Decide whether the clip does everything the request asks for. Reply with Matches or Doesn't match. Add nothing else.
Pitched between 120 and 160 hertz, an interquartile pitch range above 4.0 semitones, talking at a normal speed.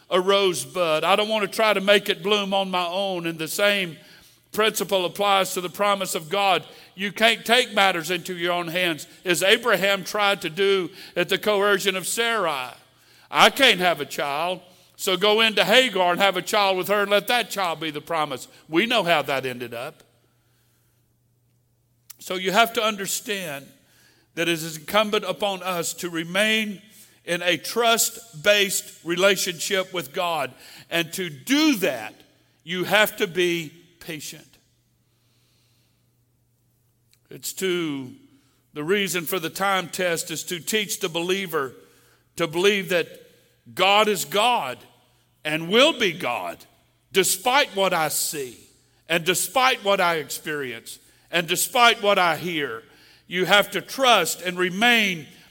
Doesn't match